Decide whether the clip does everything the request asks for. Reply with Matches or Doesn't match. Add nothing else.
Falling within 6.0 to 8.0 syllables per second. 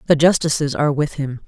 Matches